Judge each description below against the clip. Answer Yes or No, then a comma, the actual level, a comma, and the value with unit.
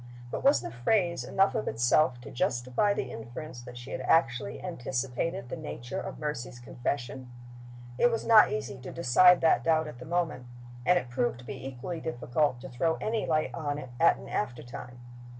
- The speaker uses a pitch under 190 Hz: Yes, low, 135 Hz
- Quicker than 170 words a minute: Yes, average, 185 wpm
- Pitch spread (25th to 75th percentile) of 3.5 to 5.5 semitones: Yes, average, 5.1 semitones